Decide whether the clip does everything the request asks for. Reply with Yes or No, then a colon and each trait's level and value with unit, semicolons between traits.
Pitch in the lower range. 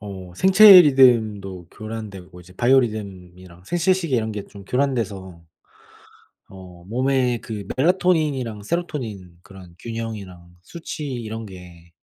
Yes: low, 110 Hz